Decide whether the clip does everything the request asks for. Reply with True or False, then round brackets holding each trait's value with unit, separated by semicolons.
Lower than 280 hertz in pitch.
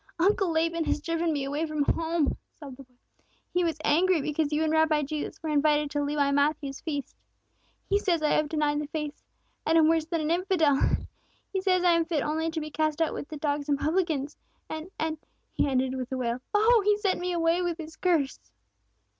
False (315 Hz)